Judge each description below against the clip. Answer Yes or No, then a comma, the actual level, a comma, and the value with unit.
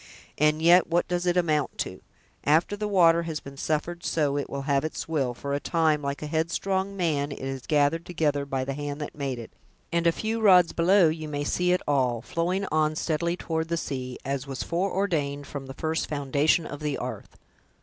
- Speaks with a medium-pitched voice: Yes, medium, 155 Hz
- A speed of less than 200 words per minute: No, fast, 205 wpm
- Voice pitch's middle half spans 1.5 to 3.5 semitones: Yes, average, 3.2 semitones